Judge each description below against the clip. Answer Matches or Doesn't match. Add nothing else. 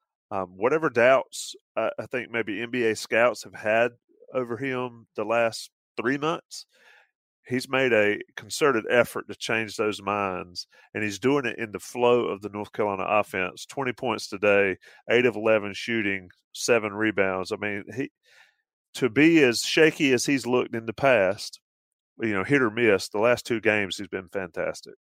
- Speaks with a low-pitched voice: Matches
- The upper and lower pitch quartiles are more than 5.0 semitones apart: Doesn't match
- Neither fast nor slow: Matches